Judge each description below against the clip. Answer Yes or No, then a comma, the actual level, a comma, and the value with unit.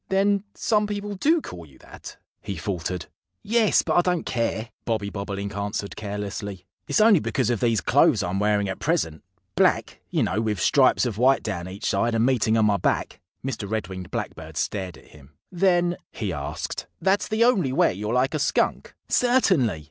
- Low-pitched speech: Yes, low, 110 Hz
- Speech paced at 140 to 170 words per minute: No, average, 185 wpm